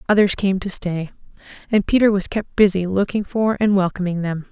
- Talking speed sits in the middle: Yes, average, 185 wpm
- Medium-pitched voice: No, high, 195 Hz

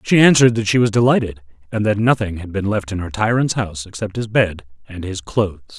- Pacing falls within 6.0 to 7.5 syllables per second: Yes, 6.2 syllables/s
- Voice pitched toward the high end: No, low, 105 Hz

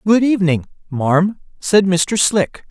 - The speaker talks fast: No, slow, 135 wpm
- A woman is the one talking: No, male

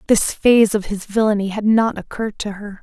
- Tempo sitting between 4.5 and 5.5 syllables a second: No, 5.7 syllables/s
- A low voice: No, high, 210 Hz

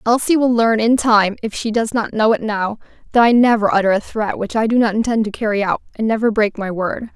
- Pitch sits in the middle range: No, high, 220 Hz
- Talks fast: Yes, fast, 260 wpm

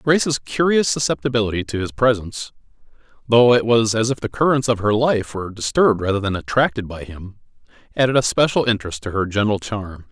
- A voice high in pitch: No, low, 115 Hz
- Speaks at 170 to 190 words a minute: Yes, average, 185 wpm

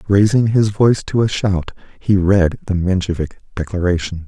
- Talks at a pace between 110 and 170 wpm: Yes, average, 155 wpm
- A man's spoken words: Yes, male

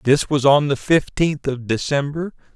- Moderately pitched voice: Yes, medium, 145 Hz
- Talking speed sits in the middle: Yes, average, 165 wpm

